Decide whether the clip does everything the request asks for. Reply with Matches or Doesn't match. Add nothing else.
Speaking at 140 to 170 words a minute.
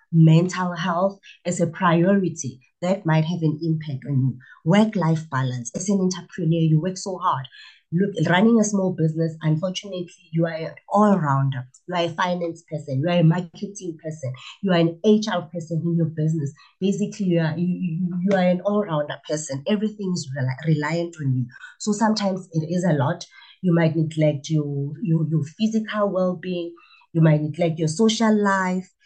Doesn't match